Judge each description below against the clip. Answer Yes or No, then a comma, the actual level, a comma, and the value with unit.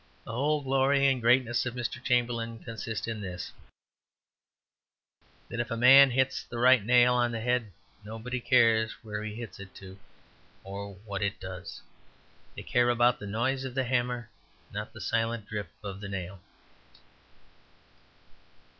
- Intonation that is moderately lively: Yes, average, 3.0 semitones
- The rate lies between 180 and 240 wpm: No, average, 155 wpm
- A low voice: Yes, low, 115 Hz